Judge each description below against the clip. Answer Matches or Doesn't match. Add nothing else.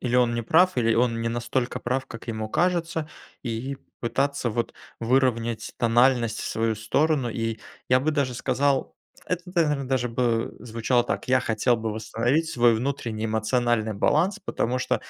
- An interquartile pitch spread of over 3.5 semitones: Doesn't match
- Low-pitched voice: Matches